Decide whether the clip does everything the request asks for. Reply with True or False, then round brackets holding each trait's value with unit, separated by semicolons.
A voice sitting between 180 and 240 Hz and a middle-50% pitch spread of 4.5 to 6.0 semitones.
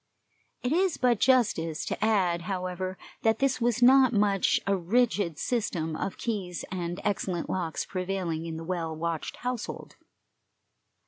True (190 Hz; 5.5 semitones)